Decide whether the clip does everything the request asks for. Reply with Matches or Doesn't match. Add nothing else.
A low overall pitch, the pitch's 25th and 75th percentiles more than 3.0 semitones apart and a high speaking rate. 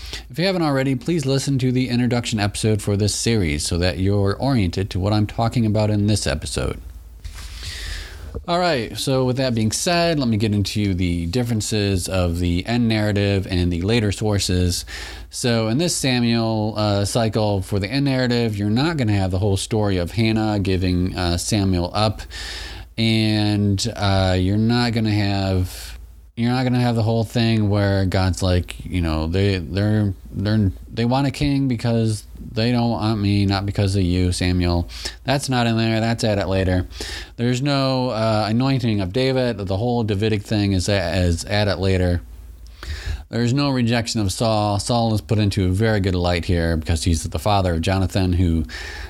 Doesn't match